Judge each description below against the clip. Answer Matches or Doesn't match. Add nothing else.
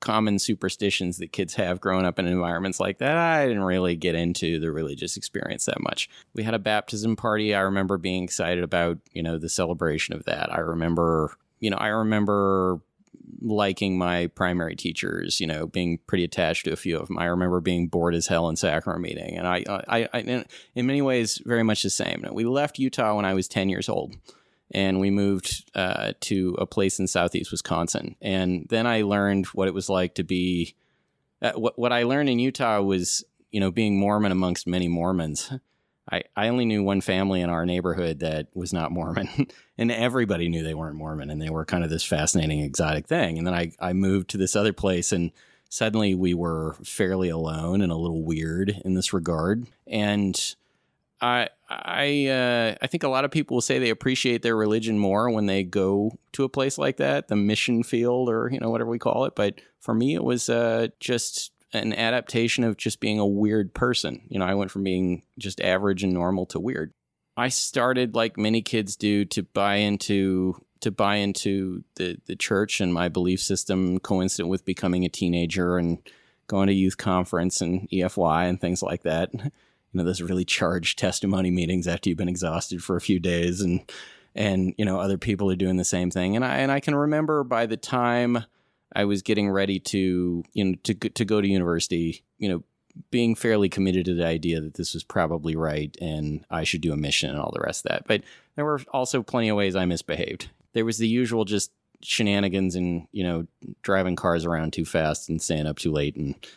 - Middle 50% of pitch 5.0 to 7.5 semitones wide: Doesn't match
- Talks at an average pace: Doesn't match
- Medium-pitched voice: Doesn't match